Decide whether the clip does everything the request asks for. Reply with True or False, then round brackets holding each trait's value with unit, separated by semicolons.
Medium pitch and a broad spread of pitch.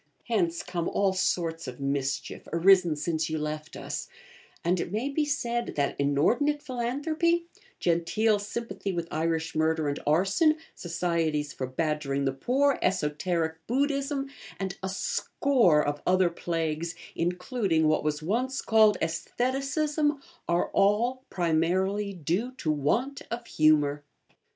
True (180 Hz; 7.3 semitones)